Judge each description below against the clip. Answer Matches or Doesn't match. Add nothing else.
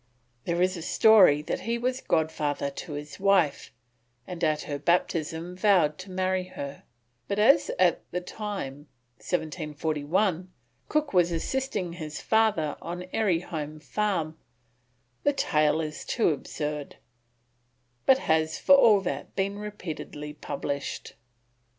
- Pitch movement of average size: Matches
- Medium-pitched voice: Matches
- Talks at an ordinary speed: Doesn't match